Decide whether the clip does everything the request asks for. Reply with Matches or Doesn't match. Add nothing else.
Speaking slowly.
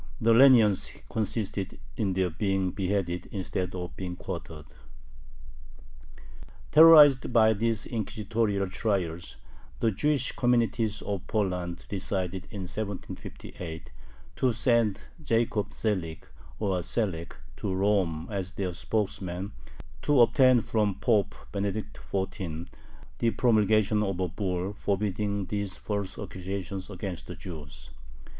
Matches